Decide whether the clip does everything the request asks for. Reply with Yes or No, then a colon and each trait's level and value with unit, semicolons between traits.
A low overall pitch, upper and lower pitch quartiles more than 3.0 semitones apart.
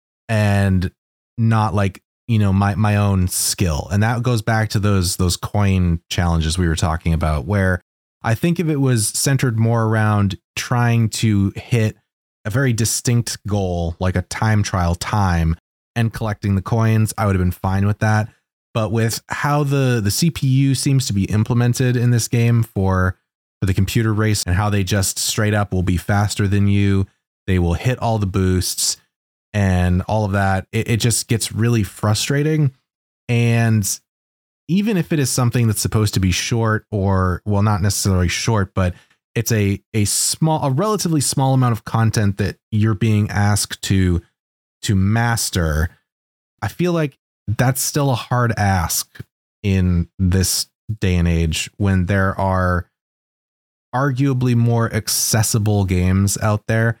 Yes: low, 105 Hz; average, 3.7 semitones